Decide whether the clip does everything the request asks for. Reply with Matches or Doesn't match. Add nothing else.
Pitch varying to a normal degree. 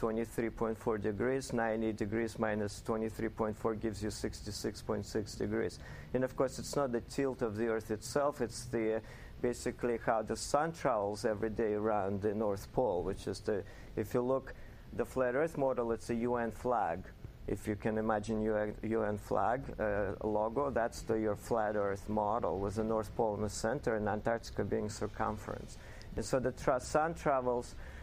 Doesn't match